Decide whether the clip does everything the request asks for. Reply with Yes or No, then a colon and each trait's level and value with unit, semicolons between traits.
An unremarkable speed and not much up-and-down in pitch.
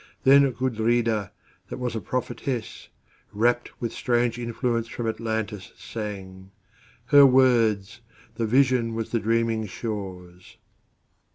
No: slow, 100 wpm; narrow, 2.3 semitones